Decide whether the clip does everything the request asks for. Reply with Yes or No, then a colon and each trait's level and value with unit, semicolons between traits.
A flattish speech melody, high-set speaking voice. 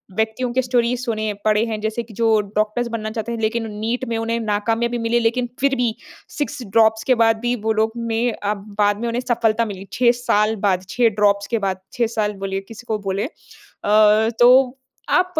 Yes: narrow, 2.1 semitones; high, 225 Hz